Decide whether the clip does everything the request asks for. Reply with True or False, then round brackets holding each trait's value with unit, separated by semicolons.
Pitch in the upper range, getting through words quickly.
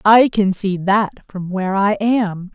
False (200 Hz; 190 wpm)